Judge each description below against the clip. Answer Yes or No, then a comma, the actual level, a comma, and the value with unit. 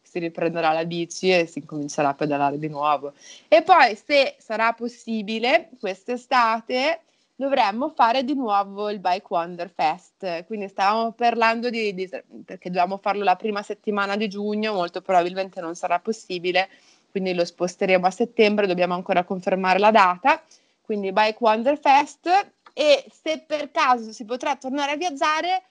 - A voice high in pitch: Yes, high, 210 Hz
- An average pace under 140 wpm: No, average, 155 wpm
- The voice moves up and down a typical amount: No, wide, 6.0 semitones